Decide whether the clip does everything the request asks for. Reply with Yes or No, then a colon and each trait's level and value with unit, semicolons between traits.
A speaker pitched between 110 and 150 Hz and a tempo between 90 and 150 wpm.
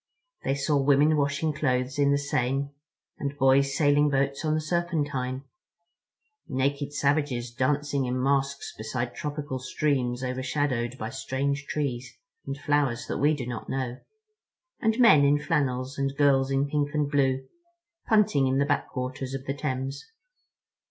Yes: medium, 140 Hz; average, 145 wpm